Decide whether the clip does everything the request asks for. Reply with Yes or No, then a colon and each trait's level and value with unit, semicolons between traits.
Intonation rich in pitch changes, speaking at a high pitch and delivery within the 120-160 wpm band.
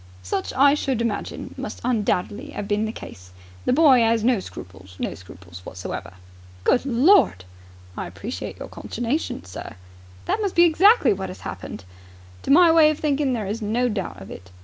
No: wide, 7.7 semitones; high, 230 Hz; average, 175 wpm